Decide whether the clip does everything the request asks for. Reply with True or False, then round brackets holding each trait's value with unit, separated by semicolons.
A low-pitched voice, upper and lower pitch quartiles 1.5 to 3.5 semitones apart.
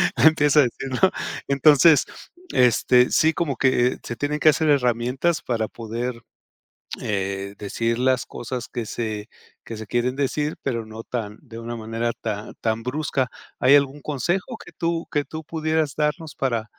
False (125 Hz; 4.5 semitones)